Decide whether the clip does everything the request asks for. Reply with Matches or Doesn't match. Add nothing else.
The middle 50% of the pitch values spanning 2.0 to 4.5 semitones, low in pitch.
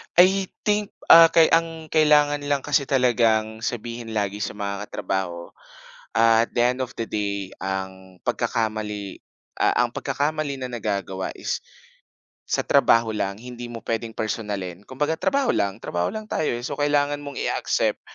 Doesn't match